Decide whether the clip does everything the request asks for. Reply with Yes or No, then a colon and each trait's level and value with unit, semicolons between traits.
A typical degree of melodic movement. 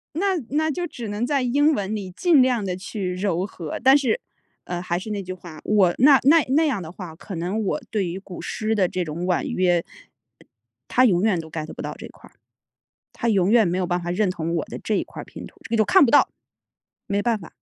No: wide, 5.8 semitones